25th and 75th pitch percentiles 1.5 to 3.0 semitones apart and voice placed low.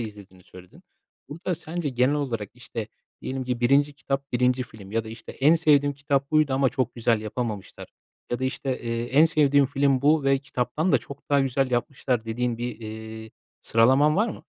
No: average, 3.7 semitones; low, 130 Hz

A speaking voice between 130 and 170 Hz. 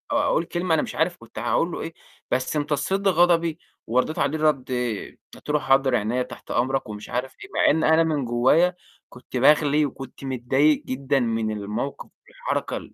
Yes: medium, 140 Hz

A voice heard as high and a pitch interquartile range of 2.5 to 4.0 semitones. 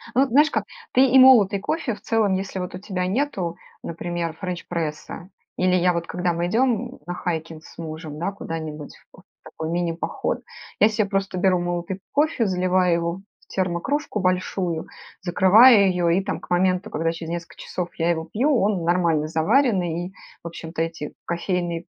No: medium, 180 Hz; average, 2.9 semitones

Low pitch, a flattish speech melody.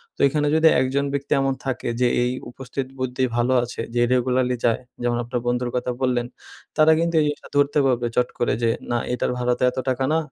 Yes: low, 125 Hz; narrow, 1.8 semitones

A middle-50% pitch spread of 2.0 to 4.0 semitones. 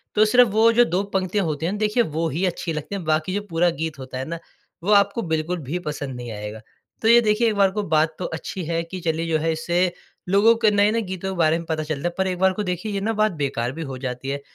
No: average, 4.6 semitones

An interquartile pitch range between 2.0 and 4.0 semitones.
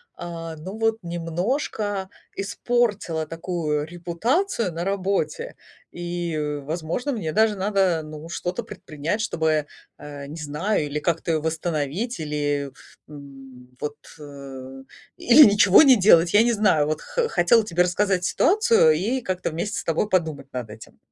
No: average, 5.3 semitones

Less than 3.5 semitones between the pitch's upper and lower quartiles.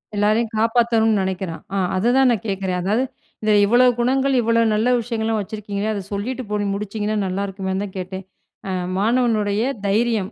Yes: average, 2.7 semitones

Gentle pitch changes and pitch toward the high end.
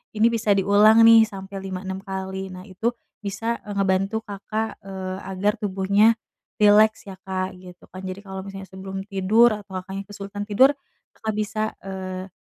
Yes: narrow, 1.9 semitones; high, 195 Hz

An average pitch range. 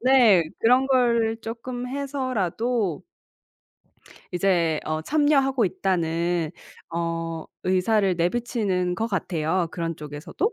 No: wide, 6.4 semitones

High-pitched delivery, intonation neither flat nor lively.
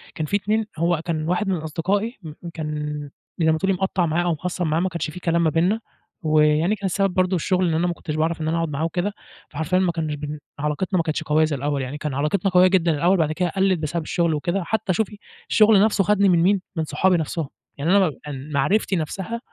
No: medium, 170 Hz; average, 3.4 semitones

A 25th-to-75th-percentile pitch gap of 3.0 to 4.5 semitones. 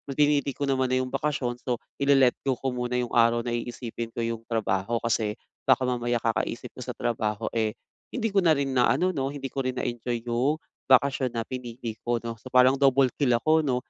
No: narrow, 2.5 semitones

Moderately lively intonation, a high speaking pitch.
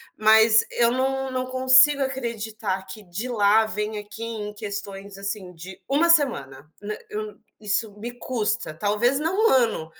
Yes: average, 3.9 semitones; high, 220 Hz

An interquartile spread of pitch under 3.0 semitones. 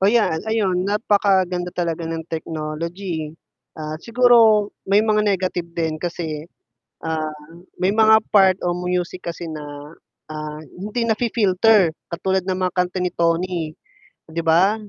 No: average, 3.7 semitones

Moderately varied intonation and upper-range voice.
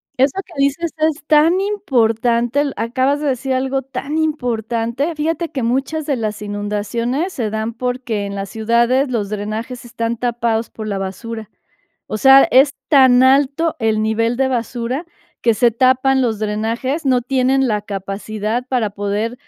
Yes: average, 3.5 semitones; high, 245 Hz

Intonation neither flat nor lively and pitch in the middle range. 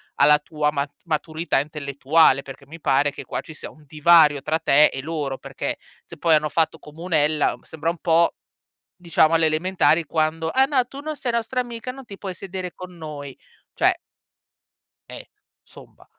Yes: average, 3.3 semitones; medium, 160 Hz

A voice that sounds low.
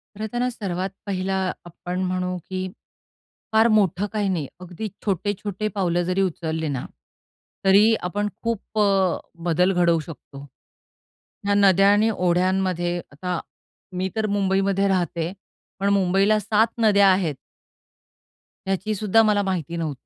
No: high, 190 Hz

